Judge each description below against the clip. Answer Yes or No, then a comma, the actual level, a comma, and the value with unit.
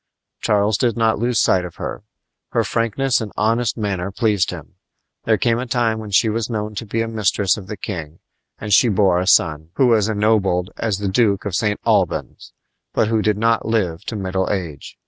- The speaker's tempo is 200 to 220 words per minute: Yes, fast, 205 wpm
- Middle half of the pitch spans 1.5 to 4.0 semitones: Yes, average, 2.8 semitones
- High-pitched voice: No, low, 105 Hz